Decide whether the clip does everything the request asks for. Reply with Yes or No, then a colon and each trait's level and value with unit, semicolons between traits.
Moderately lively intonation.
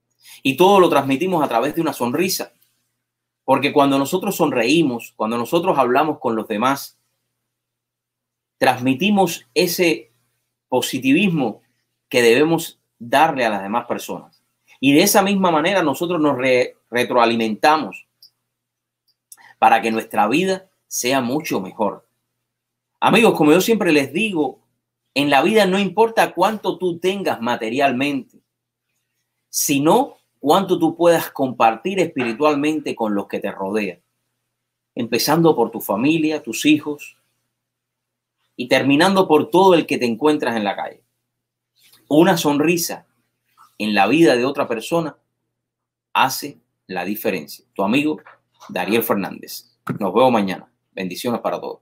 No: wide, 6.4 semitones